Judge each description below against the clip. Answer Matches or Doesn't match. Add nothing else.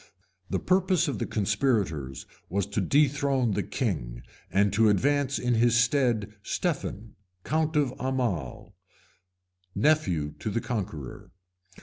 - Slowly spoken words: Matches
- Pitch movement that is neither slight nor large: Doesn't match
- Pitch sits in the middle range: Doesn't match